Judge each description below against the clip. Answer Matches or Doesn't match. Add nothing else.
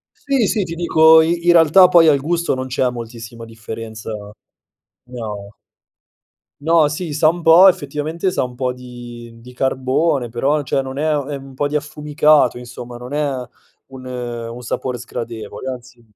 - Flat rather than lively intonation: Doesn't match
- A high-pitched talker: Doesn't match